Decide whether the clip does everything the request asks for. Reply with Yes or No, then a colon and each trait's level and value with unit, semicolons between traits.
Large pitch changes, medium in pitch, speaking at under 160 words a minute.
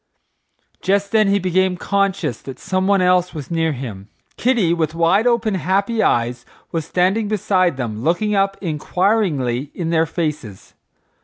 No: average, 4.6 semitones; medium, 180 Hz; average, 145 wpm